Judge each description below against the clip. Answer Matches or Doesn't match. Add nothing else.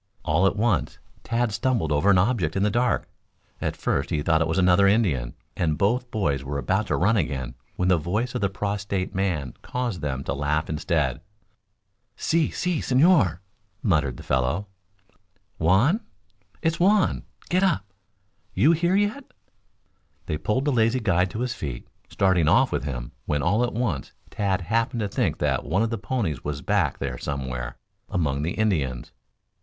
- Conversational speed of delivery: Matches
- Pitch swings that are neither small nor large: Doesn't match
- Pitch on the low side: Matches